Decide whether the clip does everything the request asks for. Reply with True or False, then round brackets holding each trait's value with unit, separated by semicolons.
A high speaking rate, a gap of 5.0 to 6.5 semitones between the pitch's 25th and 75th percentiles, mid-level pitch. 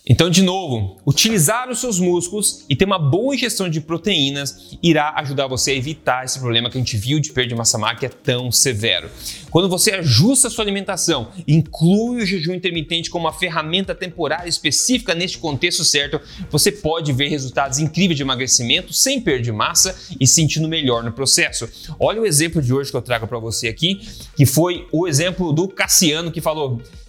True (190 wpm; 5.6 semitones; 155 Hz)